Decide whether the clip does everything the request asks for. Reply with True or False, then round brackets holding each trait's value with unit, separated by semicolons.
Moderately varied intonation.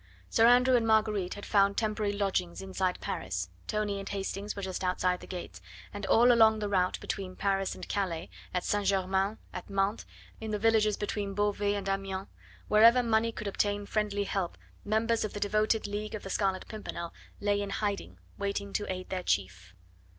False (1.8 semitones)